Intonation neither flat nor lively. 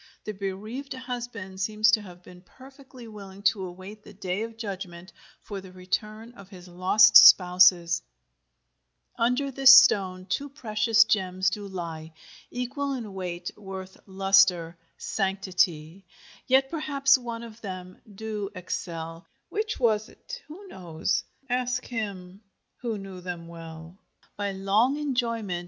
Yes: average, 4.4 semitones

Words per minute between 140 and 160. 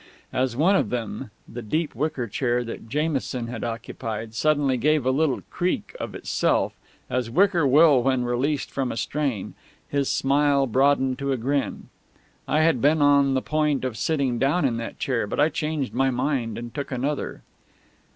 No: average, 175 wpm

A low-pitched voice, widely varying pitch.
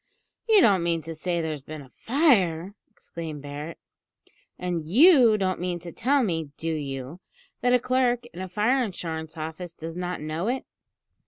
No: medium, 175 Hz; wide, 6.2 semitones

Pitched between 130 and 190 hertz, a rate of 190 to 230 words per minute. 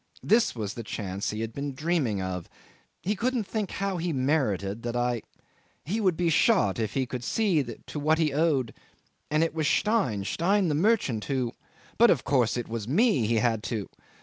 Yes: low, 135 Hz; average, 195 wpm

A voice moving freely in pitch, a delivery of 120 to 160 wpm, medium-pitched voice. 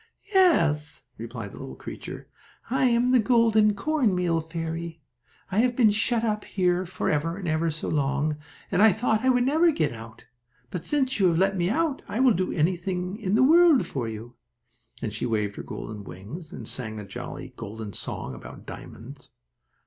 No: wide, 8.6 semitones; average, 185 wpm; medium, 180 Hz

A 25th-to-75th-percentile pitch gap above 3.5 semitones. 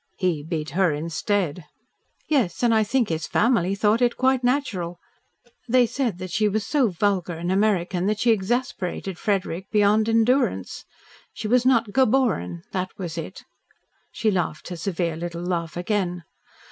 Yes: average, 4.7 semitones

